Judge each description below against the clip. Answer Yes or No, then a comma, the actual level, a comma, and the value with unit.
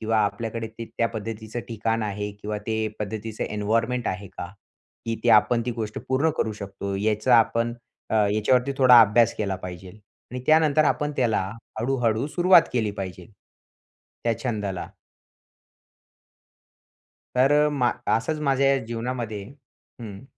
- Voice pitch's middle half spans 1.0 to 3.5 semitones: Yes, average, 3.1 semitones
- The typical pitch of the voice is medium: No, low, 115 Hz